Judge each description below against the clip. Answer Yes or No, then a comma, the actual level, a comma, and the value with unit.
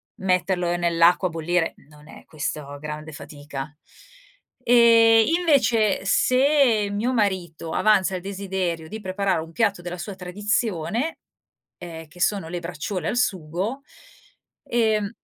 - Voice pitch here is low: No, medium, 185 Hz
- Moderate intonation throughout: Yes, average, 4.5 semitones